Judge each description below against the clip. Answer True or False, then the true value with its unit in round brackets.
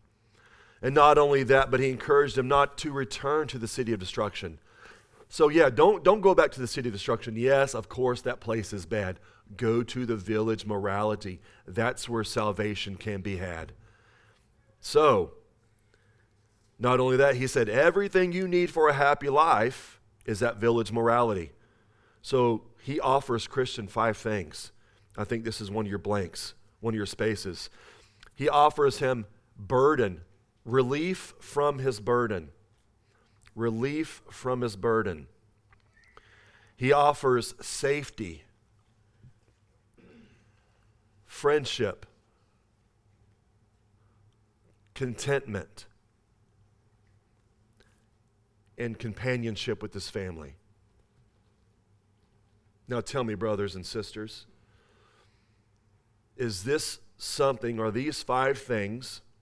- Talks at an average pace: False (115 wpm)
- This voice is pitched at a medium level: False (110 Hz)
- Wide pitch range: False (3.1 semitones)